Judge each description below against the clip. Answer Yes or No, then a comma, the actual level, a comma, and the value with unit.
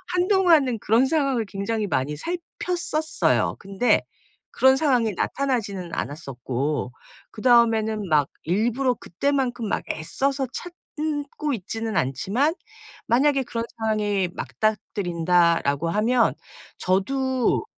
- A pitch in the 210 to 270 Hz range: Yes, high, 225 Hz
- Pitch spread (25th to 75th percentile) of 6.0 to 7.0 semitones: Yes, wide, 6.3 semitones